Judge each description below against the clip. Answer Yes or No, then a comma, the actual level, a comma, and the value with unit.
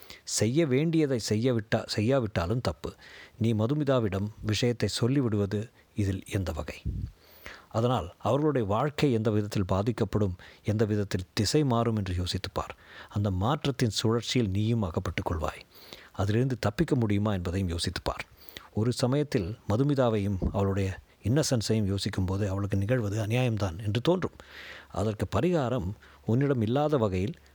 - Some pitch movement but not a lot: Yes, average, 4.1 semitones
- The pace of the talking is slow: No, average, 115 wpm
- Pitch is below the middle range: Yes, low, 110 Hz